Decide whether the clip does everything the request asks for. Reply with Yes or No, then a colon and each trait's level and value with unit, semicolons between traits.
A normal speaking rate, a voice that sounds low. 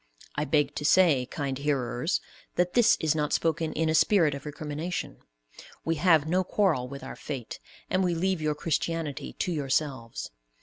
No: average, 170 wpm; medium, 155 Hz